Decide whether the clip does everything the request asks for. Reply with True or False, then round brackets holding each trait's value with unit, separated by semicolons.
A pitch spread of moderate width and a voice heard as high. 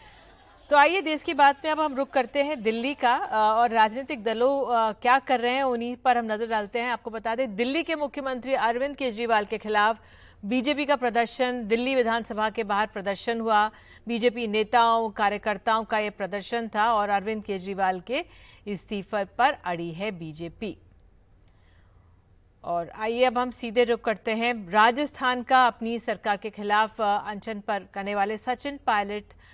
True (3.4 semitones; 225 Hz)